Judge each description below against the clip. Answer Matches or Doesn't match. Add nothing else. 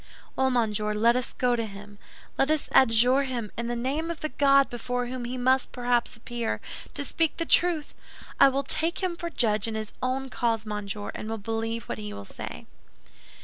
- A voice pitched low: Doesn't match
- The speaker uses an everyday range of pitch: Matches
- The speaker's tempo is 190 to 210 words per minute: Matches